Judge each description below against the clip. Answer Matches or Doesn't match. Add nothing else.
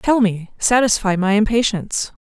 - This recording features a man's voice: Doesn't match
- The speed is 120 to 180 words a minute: Matches